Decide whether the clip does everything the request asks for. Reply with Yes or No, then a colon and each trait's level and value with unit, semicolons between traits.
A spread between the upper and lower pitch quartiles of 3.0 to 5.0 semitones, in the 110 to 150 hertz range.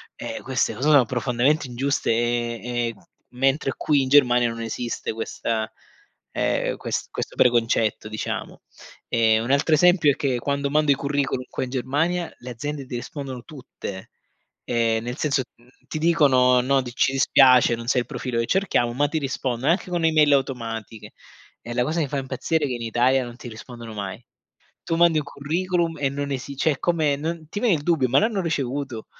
Yes: average, 3.7 semitones; low, 135 Hz